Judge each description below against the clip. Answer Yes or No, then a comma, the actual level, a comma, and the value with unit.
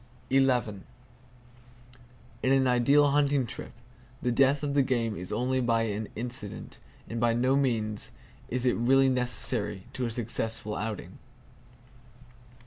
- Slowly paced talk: Yes, slow, 125 wpm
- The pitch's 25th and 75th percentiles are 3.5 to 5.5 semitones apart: No, average, 2.9 semitones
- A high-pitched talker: No, low, 125 Hz